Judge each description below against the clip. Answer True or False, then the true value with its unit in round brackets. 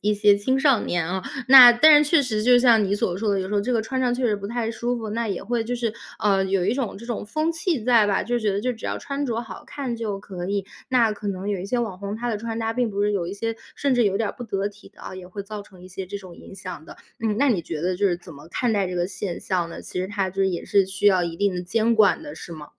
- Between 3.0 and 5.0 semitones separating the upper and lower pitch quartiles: True (3.8 semitones)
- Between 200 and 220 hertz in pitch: True (210 Hz)